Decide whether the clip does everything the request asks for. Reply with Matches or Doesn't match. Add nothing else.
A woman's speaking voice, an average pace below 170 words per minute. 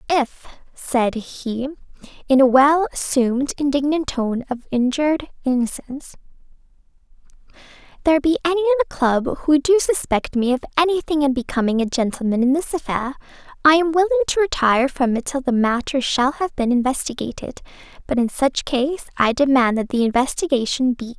Matches